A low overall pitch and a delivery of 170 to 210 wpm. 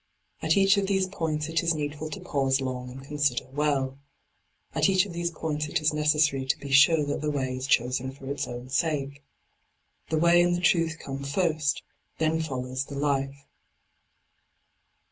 No: medium, 150 Hz; average, 180 wpm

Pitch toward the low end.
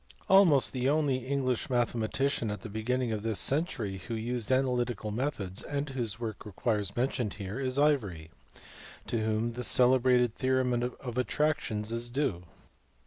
Yes: low, 120 Hz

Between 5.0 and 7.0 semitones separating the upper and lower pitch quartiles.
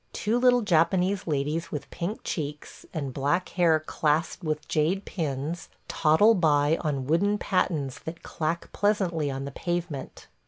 No: average, 3.7 semitones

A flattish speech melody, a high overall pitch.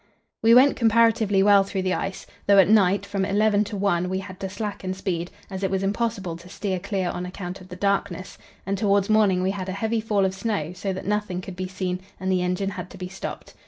Yes: narrow, 1.8 semitones; high, 195 Hz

